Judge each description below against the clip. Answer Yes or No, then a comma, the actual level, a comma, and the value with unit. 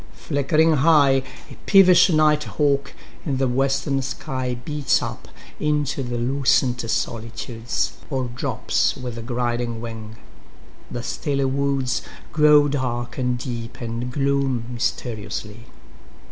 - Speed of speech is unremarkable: No, slow, 100 wpm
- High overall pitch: No, low, 130 Hz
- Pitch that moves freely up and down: No, average, 2.8 semitones